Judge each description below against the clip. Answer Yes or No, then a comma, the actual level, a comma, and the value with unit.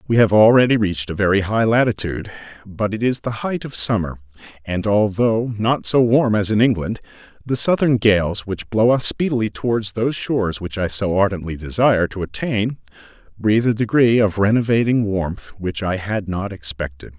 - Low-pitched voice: Yes, low, 105 Hz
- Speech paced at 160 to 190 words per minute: Yes, average, 180 wpm